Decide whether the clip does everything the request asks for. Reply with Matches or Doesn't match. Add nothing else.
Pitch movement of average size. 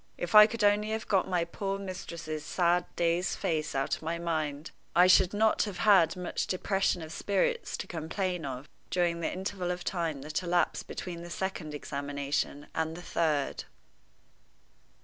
Matches